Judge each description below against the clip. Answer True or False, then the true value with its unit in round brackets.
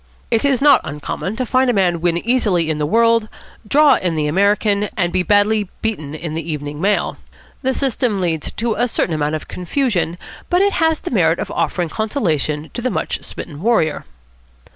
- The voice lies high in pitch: True (200 Hz)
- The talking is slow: False (190 wpm)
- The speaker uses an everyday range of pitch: False (6.6 semitones)